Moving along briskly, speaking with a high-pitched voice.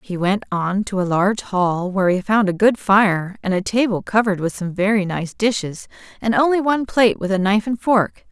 Yes: fast, 225 wpm; high, 200 Hz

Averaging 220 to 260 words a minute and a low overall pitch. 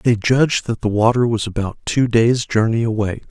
No: average, 200 wpm; low, 115 Hz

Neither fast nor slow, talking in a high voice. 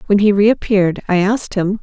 Yes: average, 195 wpm; high, 200 Hz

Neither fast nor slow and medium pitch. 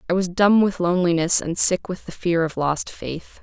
No: fast, 230 wpm; medium, 175 Hz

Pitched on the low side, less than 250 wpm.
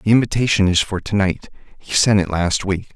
Yes: low, 100 Hz; fast, 205 wpm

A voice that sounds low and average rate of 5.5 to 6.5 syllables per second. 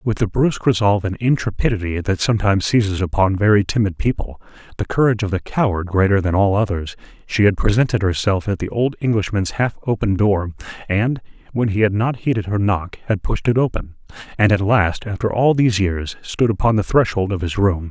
Yes: low, 105 Hz; 5.7 syllables/s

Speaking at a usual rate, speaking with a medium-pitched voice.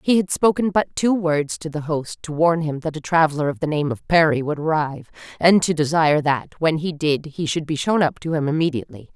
No: fast, 245 wpm; medium, 155 Hz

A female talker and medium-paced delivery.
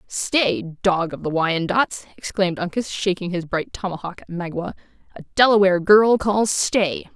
Yes: female; average, 150 wpm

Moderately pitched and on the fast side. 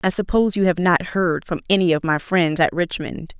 Yes: medium, 175 Hz; fast, 230 wpm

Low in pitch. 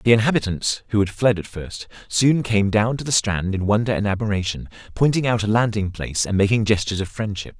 Yes: low, 105 Hz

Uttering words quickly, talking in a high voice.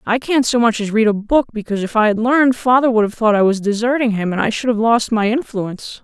Yes: fast, 280 wpm; high, 225 Hz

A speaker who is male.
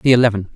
Yes: male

